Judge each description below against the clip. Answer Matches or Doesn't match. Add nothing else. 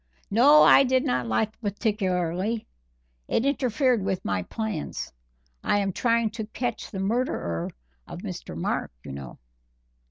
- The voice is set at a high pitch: Matches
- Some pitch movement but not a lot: Matches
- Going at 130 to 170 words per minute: Matches